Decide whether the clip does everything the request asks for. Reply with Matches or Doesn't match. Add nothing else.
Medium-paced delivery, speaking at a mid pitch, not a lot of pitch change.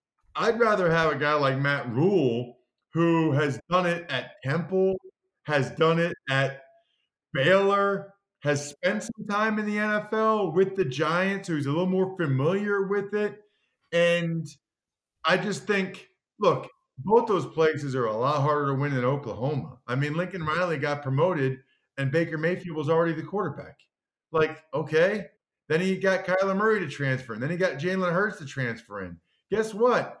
Doesn't match